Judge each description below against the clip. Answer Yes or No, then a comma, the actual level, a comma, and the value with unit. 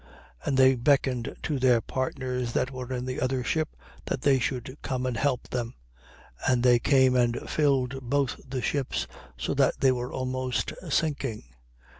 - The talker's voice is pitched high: No, low, 130 Hz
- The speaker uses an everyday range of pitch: No, narrow, 1.4 semitones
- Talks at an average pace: Yes, average, 170 wpm